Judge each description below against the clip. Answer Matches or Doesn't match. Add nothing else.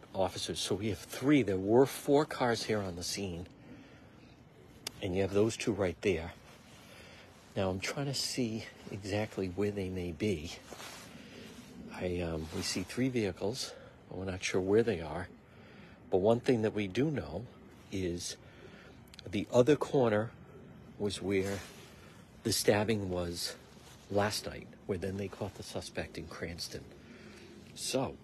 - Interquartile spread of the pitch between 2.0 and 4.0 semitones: Matches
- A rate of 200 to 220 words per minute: Doesn't match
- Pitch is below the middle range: Matches